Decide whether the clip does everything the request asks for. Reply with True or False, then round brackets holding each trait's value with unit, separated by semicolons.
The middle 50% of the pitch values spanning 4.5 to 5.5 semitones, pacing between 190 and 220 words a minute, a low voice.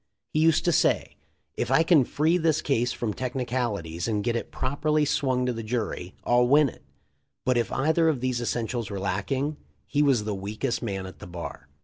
True (5.2 semitones; 205 wpm; 125 Hz)